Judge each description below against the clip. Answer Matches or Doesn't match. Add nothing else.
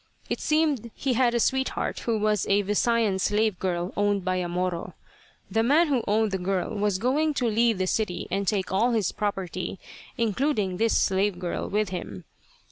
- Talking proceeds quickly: Doesn't match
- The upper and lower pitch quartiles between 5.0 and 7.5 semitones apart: Doesn't match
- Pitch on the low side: Doesn't match